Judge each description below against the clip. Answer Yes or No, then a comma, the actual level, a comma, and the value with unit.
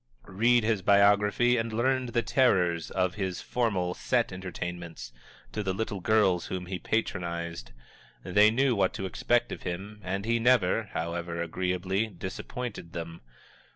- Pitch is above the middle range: No, very low, 95 Hz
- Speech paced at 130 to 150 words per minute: Yes, average, 145 wpm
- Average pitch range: Yes, average, 4.2 semitones